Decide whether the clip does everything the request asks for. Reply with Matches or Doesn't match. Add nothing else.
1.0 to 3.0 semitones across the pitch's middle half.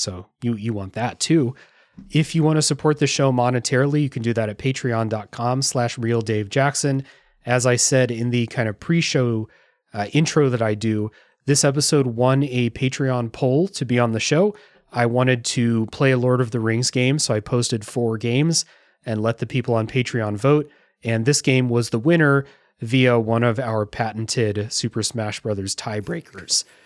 Doesn't match